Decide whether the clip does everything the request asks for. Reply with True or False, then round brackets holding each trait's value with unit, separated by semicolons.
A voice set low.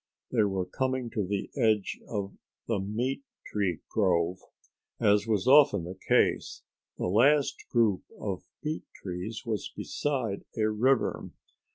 True (110 Hz)